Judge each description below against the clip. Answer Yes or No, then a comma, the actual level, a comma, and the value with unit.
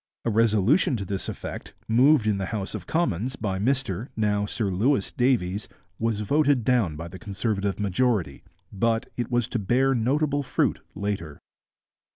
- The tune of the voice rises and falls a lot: No, average, 4.4 semitones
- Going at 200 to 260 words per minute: No, average, 160 wpm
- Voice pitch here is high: No, low, 110 Hz